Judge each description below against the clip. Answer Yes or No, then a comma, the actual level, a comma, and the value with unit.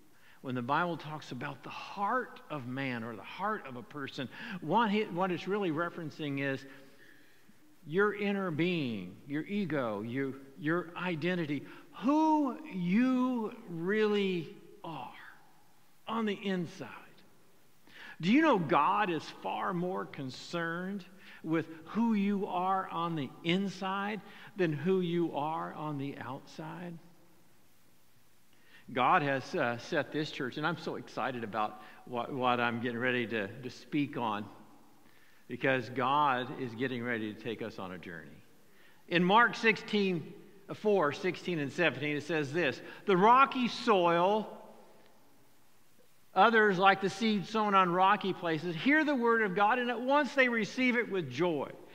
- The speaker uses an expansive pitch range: Yes, wide, 6.6 semitones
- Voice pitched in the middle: Yes, medium, 175 Hz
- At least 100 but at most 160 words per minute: Yes, slow, 135 wpm